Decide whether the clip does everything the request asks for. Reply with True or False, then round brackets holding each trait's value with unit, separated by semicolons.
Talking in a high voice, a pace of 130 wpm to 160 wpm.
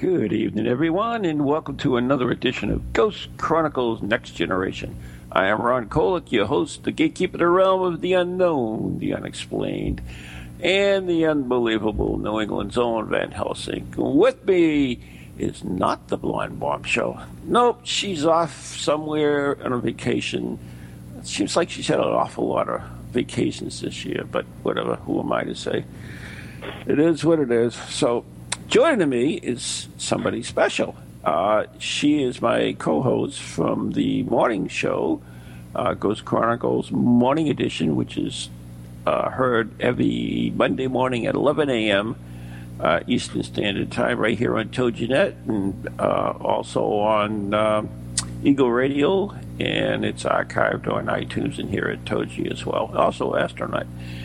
False (115 Hz; 150 wpm)